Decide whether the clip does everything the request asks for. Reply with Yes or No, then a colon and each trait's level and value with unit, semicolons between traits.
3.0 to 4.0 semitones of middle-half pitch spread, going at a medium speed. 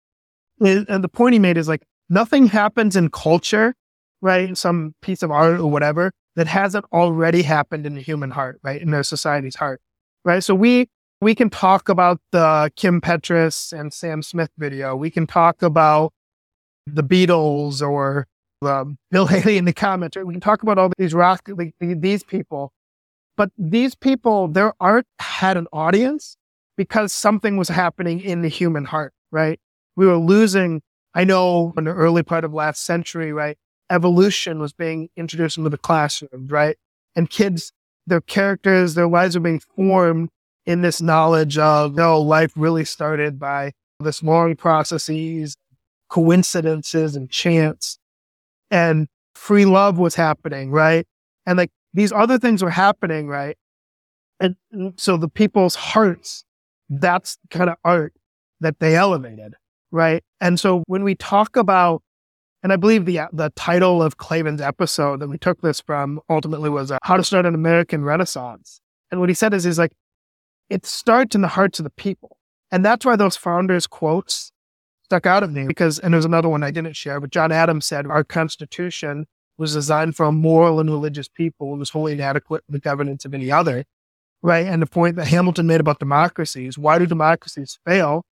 Yes: average, 3.4 semitones; average, 175 wpm